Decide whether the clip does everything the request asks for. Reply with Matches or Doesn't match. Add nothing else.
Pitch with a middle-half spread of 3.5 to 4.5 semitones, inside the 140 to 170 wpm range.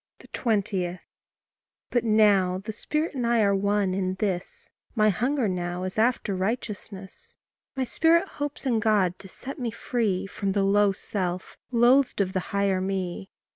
Matches